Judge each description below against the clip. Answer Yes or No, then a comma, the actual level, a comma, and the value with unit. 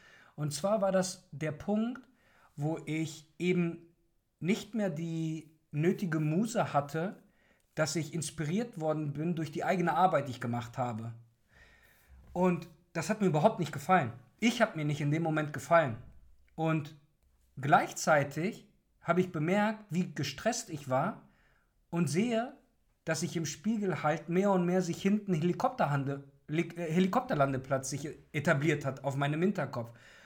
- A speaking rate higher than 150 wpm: No, average, 145 wpm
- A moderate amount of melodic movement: Yes, average, 4.1 semitones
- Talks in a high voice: No, medium, 165 Hz